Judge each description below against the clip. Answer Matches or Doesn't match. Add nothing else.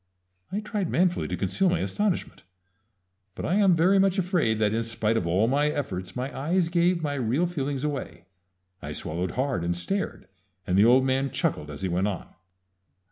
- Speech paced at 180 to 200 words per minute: Matches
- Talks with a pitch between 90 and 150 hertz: Matches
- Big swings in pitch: Matches